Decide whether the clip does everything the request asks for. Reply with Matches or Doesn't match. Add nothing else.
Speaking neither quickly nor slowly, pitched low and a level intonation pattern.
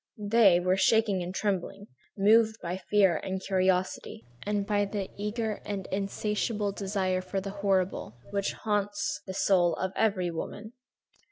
Doesn't match